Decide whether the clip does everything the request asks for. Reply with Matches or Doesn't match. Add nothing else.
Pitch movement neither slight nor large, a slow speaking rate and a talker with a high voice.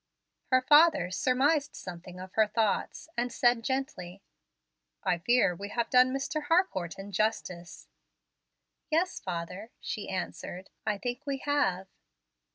Doesn't match